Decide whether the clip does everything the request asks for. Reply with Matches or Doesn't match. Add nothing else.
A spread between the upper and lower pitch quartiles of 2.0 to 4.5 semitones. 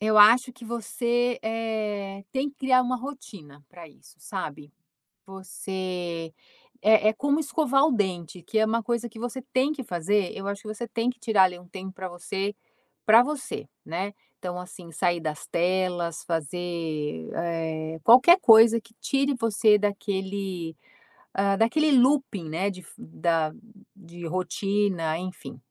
Doesn't match